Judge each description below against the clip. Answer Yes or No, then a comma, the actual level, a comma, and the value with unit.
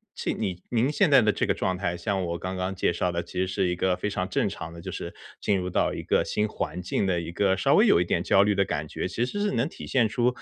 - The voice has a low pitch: Yes, very low, 95 Hz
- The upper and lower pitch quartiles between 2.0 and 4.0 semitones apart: Yes, average, 3.2 semitones